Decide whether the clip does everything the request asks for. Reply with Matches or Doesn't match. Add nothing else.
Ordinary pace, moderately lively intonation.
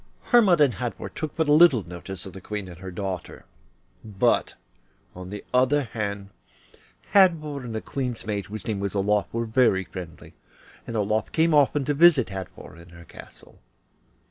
Doesn't match